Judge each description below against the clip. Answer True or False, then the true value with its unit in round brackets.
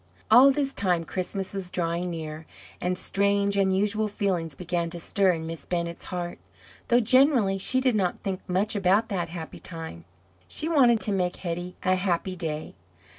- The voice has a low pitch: False (185 Hz)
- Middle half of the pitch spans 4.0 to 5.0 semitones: False (3.1 semitones)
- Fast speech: False (170 wpm)